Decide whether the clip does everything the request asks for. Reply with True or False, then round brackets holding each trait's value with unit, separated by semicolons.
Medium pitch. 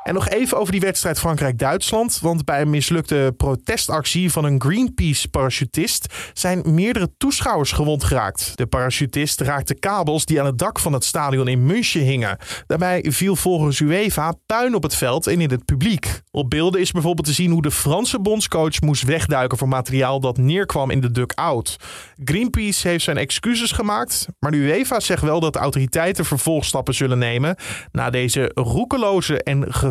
True (150 Hz)